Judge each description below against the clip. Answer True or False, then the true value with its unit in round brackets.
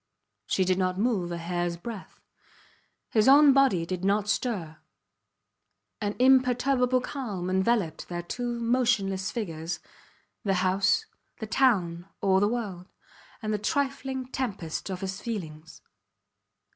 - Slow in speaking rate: True (125 wpm)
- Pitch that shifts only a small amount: False (5.2 semitones)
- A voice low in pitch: False (200 Hz)